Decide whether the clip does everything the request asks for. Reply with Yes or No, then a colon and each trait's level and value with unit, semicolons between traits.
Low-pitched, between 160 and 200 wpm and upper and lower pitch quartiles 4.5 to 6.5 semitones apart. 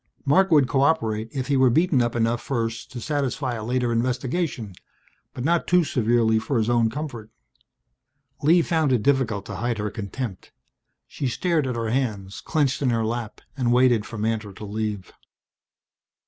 No: low, 120 Hz; average, 170 wpm; average, 3.8 semitones